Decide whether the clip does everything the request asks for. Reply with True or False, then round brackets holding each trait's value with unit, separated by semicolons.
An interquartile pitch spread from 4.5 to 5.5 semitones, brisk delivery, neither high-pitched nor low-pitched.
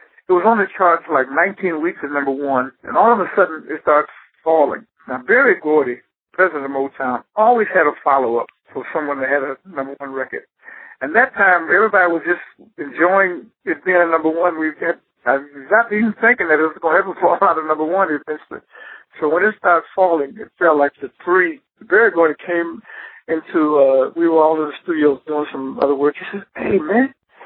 True (4.8 semitones; 220 wpm; 160 Hz)